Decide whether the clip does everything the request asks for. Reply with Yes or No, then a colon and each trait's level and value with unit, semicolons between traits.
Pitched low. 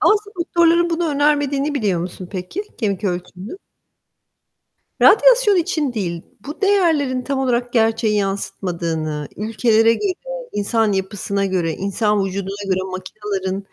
No: high, 215 Hz